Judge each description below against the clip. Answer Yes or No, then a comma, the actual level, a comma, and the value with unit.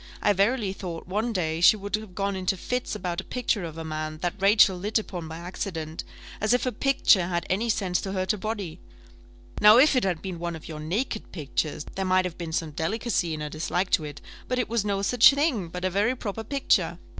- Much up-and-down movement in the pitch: No, average, 4.2 semitones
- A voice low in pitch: No, high, 190 Hz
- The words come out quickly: Yes, fast, 230 wpm